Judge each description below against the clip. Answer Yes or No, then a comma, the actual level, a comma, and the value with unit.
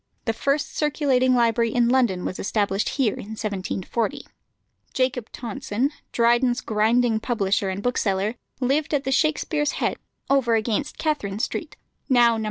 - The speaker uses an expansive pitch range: No, average, 3.8 semitones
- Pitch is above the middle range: Yes, high, 240 Hz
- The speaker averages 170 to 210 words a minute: No, average, 140 wpm